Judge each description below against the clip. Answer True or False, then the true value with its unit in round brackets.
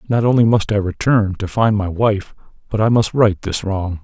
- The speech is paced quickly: True (225 wpm)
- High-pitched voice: False (105 Hz)